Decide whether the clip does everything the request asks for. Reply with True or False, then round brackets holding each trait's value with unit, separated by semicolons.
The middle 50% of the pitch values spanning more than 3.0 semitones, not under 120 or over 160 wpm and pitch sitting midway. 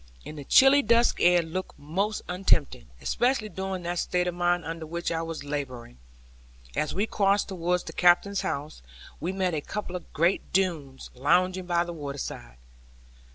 False (3.6 semitones; 170 wpm; 175 Hz)